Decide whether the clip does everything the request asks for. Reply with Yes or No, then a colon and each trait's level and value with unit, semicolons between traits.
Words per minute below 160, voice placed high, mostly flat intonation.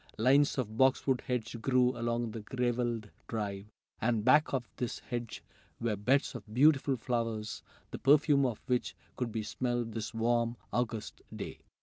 No: average, 150 wpm; low, 120 Hz; narrow, 2.2 semitones